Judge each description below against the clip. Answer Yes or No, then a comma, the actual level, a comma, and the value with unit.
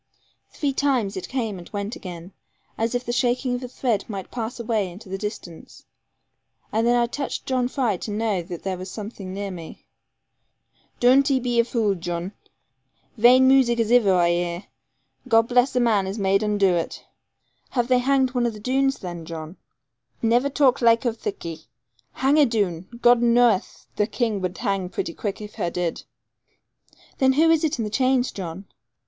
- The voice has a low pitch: No, high, 225 Hz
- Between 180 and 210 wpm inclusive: Yes, average, 190 wpm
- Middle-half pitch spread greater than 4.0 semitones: Yes, average, 4.5 semitones